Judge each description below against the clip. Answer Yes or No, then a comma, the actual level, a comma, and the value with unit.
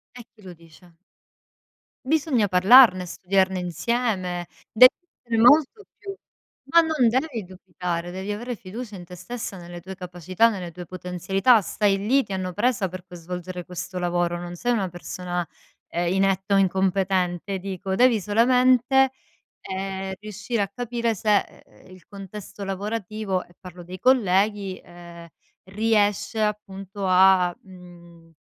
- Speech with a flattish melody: No, average, 3.5 semitones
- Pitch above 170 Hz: Yes, high, 190 Hz